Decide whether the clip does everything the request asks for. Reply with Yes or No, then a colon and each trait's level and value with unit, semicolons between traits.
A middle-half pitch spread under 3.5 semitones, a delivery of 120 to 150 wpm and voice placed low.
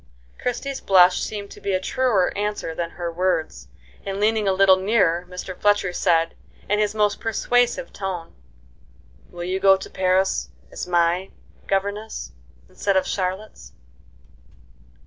No: average, 2.7 semitones; average, 140 wpm; high, 190 Hz